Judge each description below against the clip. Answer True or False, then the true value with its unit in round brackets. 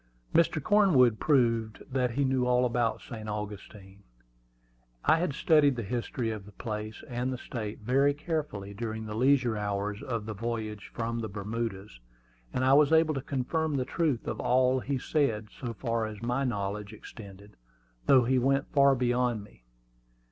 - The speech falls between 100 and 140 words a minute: False (170 wpm)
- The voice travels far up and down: False (4.0 semitones)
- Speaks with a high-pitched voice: False (120 Hz)